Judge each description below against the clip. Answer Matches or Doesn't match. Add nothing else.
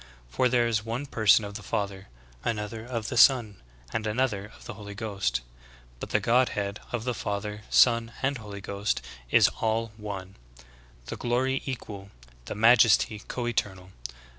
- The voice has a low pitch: Matches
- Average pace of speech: Matches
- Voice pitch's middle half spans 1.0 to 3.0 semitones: Matches